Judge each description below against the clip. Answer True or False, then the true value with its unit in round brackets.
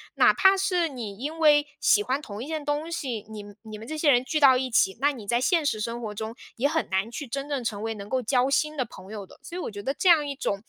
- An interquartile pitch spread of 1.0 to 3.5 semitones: False (5.4 semitones)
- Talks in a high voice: True (260 Hz)